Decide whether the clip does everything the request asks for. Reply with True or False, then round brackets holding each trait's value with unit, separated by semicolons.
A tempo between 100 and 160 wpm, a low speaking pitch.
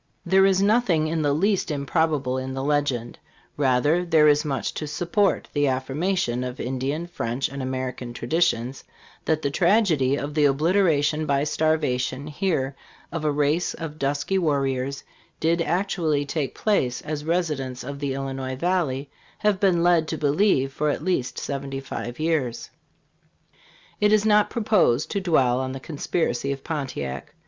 False (155 wpm; 145 Hz)